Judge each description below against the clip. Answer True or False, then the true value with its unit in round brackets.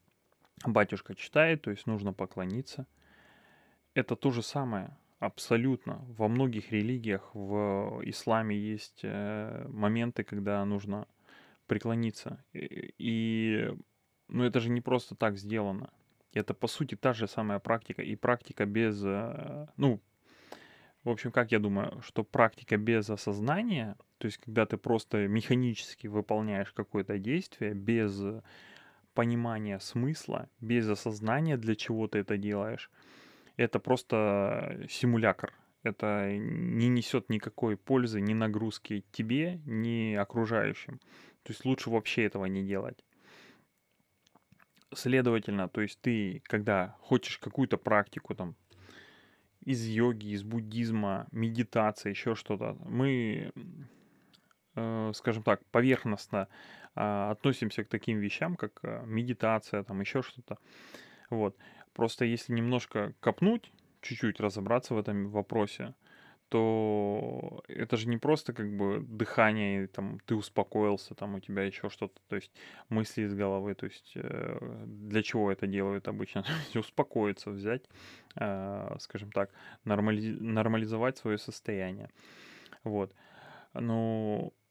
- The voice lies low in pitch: True (110 Hz)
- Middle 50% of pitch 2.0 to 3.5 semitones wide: True (2.7 semitones)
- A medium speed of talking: True (120 wpm)